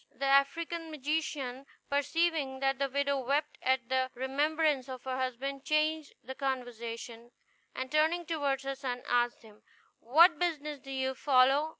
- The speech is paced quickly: No, average, 150 wpm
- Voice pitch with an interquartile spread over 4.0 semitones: No, average, 2.8 semitones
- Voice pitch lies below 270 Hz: No, very high, 275 Hz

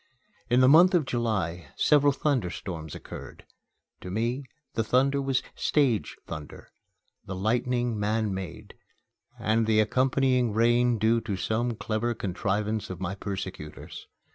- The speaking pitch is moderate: No, low, 115 Hz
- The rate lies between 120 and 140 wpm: Yes, slow, 135 wpm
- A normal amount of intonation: Yes, average, 4.3 semitones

